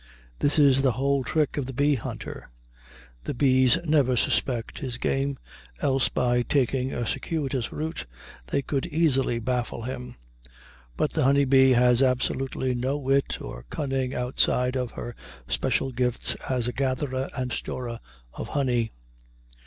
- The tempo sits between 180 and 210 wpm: No, average, 145 wpm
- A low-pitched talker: Yes, low, 130 Hz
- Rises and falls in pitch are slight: Yes, narrow, 1.9 semitones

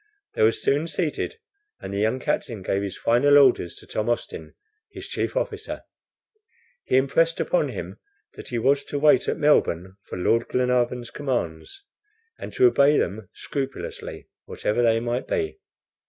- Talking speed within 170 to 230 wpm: No, average, 155 wpm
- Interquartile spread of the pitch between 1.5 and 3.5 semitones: No, average, 5.3 semitones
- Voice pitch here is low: Yes, low, 125 Hz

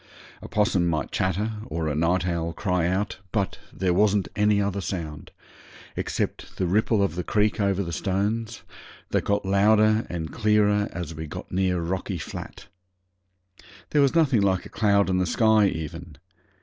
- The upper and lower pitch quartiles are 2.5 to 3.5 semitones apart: Yes, average, 3.2 semitones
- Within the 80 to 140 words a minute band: No, average, 165 wpm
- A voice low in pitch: Yes, very low, 95 Hz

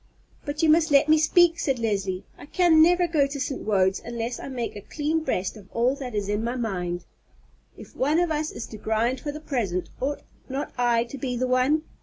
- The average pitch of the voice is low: No, very high, 255 Hz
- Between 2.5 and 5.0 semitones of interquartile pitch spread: No, wide, 5.4 semitones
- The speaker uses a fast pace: Yes, fast, 225 wpm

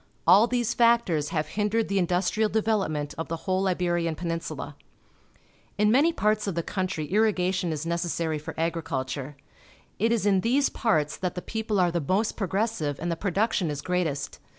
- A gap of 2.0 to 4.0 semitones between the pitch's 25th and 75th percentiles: No, average, 4.5 semitones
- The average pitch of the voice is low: No, medium, 185 Hz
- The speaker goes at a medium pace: Yes, average, 180 wpm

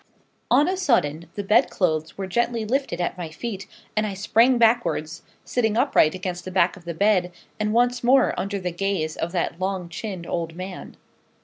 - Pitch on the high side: Yes, high, 195 Hz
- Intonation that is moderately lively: Yes, average, 4.9 semitones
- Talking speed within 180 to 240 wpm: Yes, average, 190 wpm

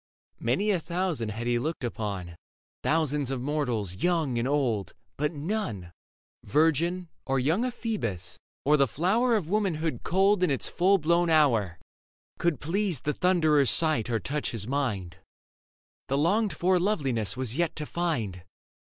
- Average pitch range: No, wide, 6.6 semitones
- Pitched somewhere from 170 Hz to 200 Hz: No, medium, 150 Hz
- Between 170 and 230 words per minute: No, average, 155 wpm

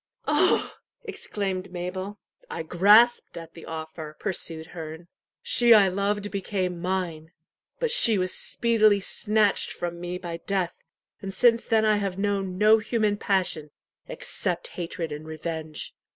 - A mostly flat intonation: No, average, 3.5 semitones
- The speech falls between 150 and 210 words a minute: No, slow, 135 wpm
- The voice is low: No, medium, 185 Hz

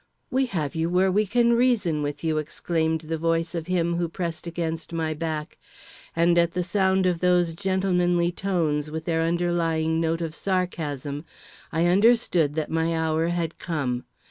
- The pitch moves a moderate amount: No, narrow, 2.0 semitones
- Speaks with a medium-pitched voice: Yes, medium, 165 Hz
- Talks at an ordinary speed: Yes, average, 170 wpm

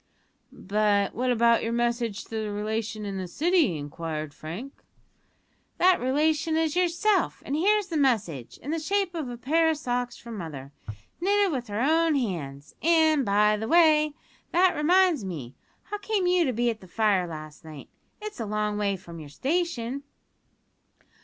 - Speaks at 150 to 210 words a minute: Yes, average, 170 wpm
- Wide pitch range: Yes, wide, 8.2 semitones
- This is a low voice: No, high, 240 Hz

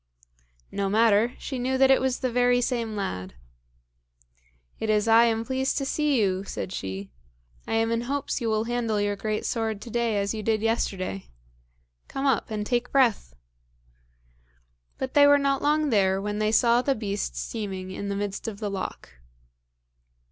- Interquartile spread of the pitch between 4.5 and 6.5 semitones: No, average, 3.5 semitones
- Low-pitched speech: No, high, 225 Hz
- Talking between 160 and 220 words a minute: Yes, average, 175 wpm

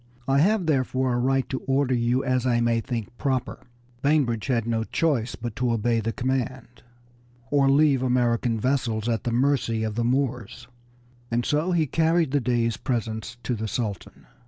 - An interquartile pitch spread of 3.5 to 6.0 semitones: No, average, 2.7 semitones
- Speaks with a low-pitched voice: Yes, low, 125 Hz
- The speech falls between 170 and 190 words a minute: Yes, average, 180 wpm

